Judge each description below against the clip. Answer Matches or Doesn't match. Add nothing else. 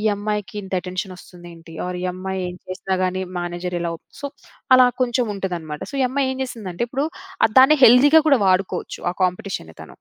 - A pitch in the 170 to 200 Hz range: Matches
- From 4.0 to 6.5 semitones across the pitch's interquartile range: Matches